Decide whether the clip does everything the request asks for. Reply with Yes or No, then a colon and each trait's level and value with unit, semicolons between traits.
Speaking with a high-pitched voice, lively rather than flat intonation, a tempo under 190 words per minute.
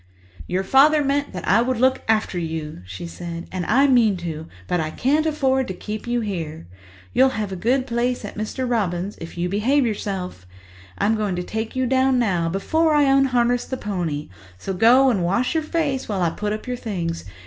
No: high, 215 Hz; wide, 6.5 semitones; fast, 205 wpm